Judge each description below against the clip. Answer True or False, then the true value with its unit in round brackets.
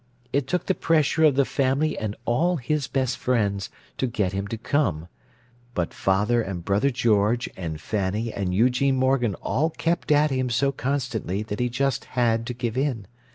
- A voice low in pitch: True (120 Hz)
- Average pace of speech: True (175 wpm)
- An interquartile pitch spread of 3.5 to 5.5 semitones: True (4.6 semitones)